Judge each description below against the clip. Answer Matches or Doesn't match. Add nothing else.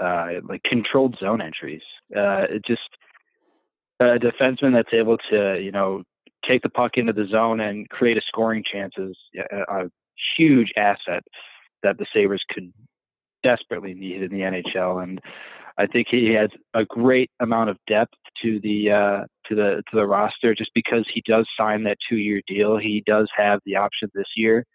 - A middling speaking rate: Matches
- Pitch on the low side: Matches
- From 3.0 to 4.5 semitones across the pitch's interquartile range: Doesn't match